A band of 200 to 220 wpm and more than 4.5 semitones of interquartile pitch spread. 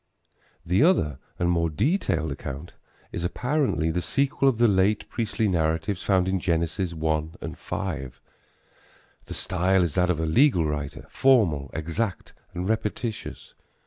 No: average, 145 wpm; average, 5.1 semitones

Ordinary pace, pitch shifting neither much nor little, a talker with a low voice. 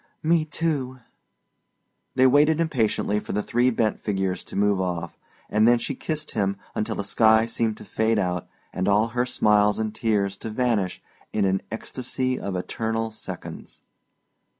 Yes: average, 160 wpm; average, 3.7 semitones; low, 110 Hz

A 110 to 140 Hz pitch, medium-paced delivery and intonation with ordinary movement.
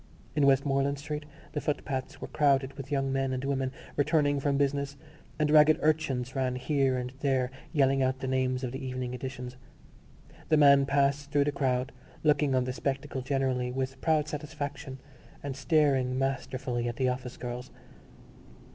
No: low, 135 Hz; average, 165 wpm; narrow, 1.8 semitones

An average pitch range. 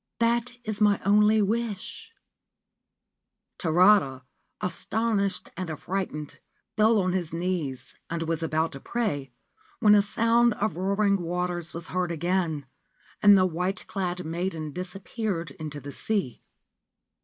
Yes: average, 4.1 semitones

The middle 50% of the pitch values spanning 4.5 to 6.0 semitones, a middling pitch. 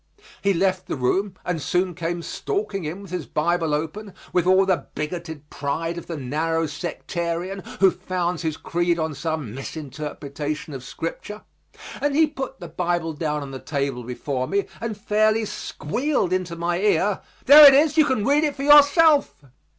Yes: average, 4.9 semitones; medium, 175 Hz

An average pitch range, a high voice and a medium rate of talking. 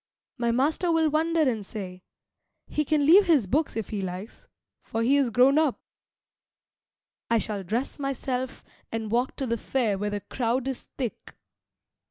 Yes: average, 4.7 semitones; very high, 250 Hz; average, 165 wpm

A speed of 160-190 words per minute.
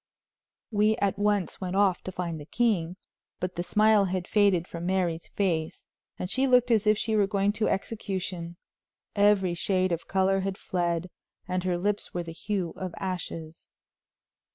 Yes: average, 170 wpm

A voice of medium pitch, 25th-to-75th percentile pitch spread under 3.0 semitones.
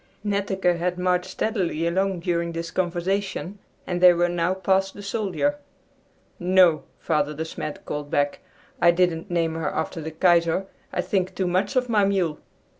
Yes: medium, 180 Hz; narrow, 2.5 semitones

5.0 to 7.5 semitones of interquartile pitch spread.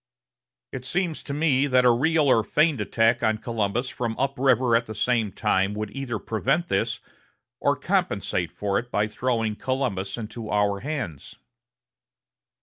No: average, 4.0 semitones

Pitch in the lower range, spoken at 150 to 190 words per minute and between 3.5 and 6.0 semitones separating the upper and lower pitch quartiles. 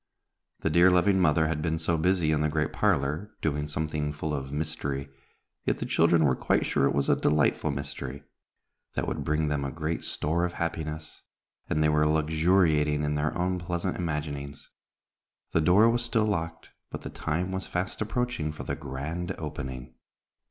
No: very low, 80 Hz; average, 180 wpm; average, 2.8 semitones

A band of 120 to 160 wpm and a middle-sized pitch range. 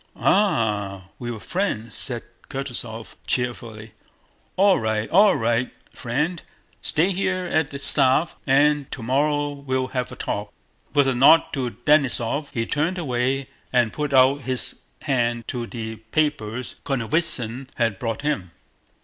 Yes: slow, 135 wpm; average, 4.2 semitones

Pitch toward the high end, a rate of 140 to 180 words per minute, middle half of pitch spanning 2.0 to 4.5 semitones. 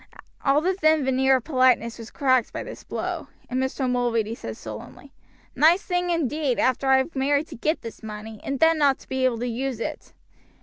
No: very high, 265 Hz; fast, 205 wpm; average, 3.8 semitones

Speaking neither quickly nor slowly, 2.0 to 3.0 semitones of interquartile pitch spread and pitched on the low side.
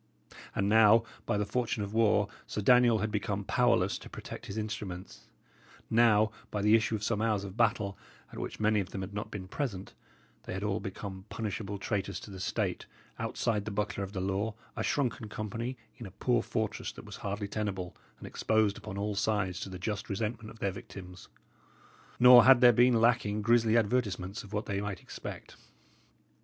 Yes: average, 190 wpm; narrow, 2.4 semitones; low, 105 Hz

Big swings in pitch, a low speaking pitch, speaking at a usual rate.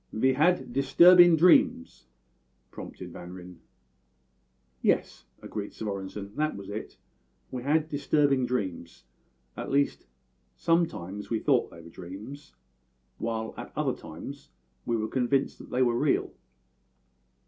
No: wide, 6.8 semitones; low, 125 Hz; slow, 125 wpm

